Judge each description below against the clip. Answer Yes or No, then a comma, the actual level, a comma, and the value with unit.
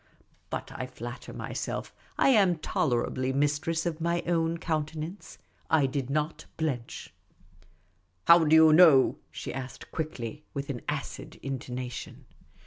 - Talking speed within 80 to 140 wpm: Yes, slow, 135 wpm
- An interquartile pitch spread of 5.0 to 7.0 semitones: No, average, 3.6 semitones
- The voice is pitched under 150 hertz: No, medium, 155 Hz